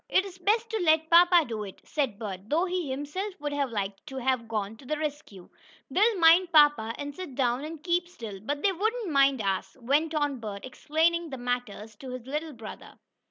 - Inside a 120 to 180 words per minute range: No, average, 200 wpm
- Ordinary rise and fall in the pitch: No, wide, 6.5 semitones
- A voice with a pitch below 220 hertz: No, very high, 290 Hz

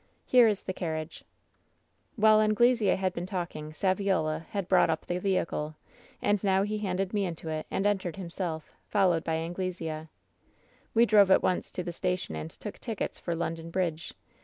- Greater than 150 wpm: Yes, average, 170 wpm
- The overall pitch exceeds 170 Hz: Yes, medium, 185 Hz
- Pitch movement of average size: Yes, average, 3.5 semitones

